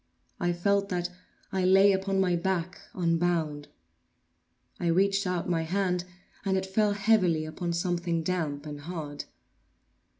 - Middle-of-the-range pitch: Yes, medium, 180 Hz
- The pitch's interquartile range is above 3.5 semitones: No, narrow, 2.4 semitones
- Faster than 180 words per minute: No, slow, 135 wpm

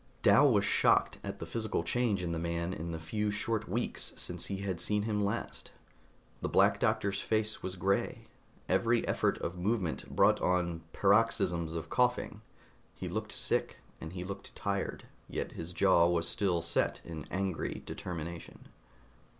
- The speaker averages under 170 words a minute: Yes, average, 160 wpm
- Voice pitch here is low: Yes, very low, 95 Hz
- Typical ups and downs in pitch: Yes, average, 3.7 semitones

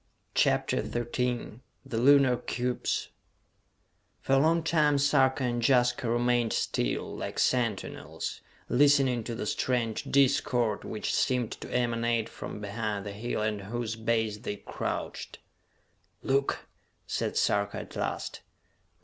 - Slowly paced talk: Yes, slow, 125 wpm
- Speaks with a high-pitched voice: No, low, 120 Hz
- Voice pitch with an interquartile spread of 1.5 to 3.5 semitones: Yes, average, 2.9 semitones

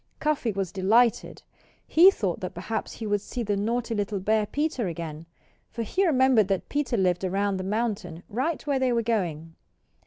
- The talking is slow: No, average, 180 wpm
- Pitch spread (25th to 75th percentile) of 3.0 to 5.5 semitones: Yes, average, 4.4 semitones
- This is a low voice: No, high, 215 Hz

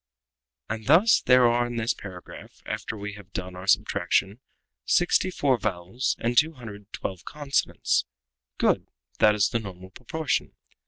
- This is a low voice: Yes, low, 110 Hz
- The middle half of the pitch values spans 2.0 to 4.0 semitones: No, average, 4.8 semitones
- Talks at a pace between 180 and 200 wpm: No, average, 155 wpm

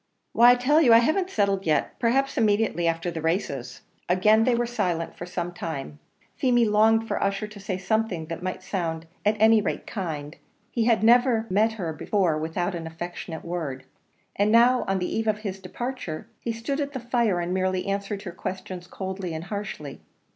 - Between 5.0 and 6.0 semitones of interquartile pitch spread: No, average, 4.5 semitones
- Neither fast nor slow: Yes, average, 190 wpm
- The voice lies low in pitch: No, high, 195 Hz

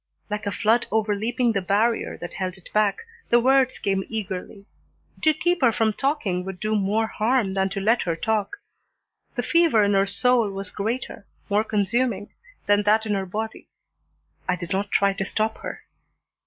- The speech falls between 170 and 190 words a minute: Yes, average, 180 wpm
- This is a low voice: No, high, 210 Hz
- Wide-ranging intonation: No, average, 2.7 semitones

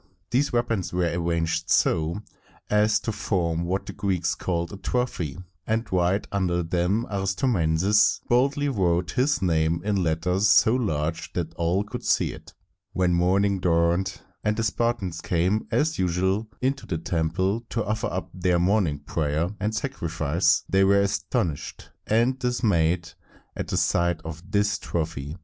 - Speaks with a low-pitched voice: Yes, very low, 95 Hz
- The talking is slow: No, average, 150 wpm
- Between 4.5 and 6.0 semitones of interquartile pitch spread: No, average, 4.0 semitones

